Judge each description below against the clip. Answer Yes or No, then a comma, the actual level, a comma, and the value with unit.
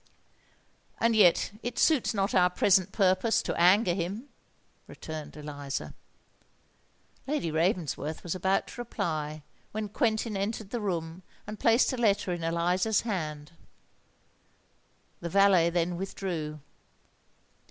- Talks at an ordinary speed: No, slow, 120 wpm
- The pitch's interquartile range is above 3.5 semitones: Yes, average, 4.2 semitones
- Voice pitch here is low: No, medium, 185 Hz